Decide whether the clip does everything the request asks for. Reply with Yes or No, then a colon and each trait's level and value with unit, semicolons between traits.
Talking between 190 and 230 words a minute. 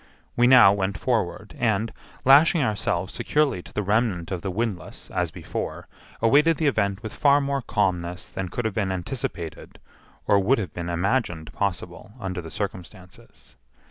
No: average, 160 wpm